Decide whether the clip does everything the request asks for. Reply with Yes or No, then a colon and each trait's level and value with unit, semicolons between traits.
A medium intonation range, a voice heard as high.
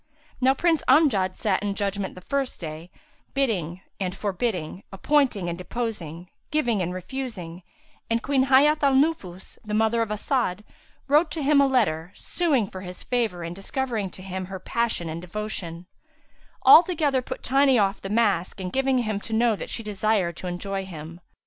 No: wide, 6.4 semitones; high, 210 Hz